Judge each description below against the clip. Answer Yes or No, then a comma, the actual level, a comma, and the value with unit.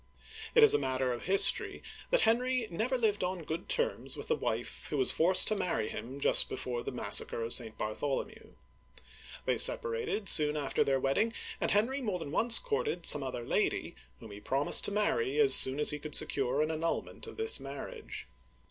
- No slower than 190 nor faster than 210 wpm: Yes, average, 195 wpm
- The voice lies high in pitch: No, medium, 170 Hz